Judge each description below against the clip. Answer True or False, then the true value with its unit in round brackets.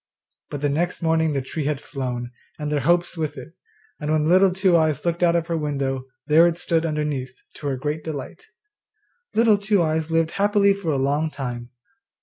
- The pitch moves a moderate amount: True (3.1 semitones)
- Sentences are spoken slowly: False (195 wpm)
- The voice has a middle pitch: True (155 Hz)